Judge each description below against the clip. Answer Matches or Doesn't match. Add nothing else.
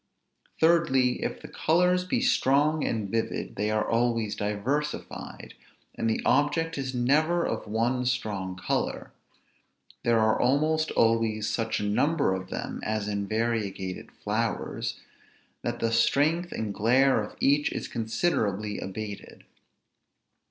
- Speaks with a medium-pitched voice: Doesn't match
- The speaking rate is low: Matches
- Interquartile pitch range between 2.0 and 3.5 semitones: Doesn't match